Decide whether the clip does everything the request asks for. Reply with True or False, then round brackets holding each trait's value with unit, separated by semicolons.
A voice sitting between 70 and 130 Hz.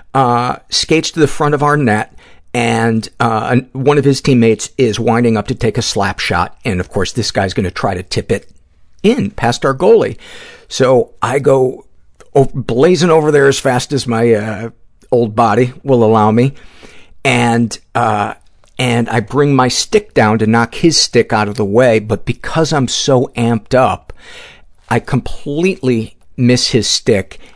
True (120 Hz)